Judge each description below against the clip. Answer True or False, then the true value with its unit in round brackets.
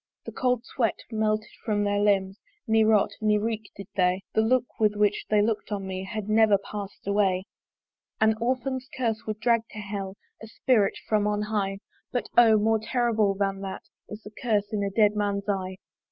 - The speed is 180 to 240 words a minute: True (190 wpm)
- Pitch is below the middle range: False (210 Hz)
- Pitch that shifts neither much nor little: False (1.8 semitones)